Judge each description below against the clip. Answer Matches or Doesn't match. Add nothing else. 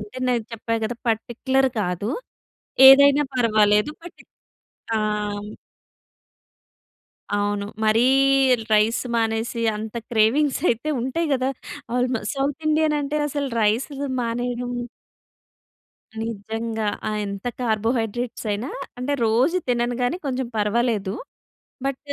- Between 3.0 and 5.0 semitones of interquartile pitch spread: Matches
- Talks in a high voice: Matches